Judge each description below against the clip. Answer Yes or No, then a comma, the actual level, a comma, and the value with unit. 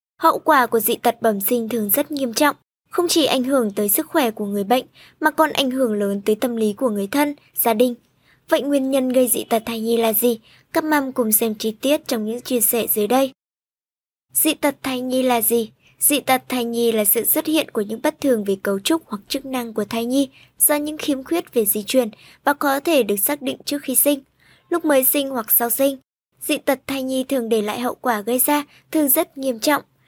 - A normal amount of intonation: Yes, average, 3.9 semitones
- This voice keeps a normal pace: Yes, average, 240 wpm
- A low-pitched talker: No, very high, 260 Hz